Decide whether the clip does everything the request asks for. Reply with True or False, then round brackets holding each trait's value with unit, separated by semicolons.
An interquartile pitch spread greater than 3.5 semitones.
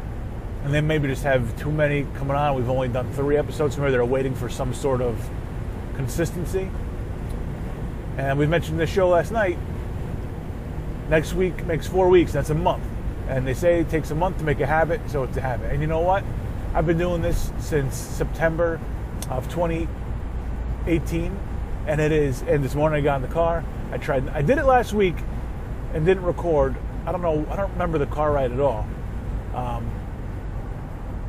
True (5.1 semitones)